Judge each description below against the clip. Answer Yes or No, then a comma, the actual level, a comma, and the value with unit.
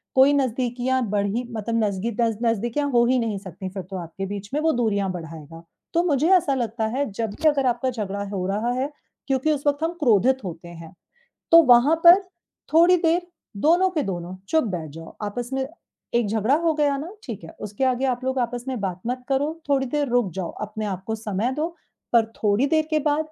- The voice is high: Yes, high, 240 Hz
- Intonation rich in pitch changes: Yes, wide, 5.7 semitones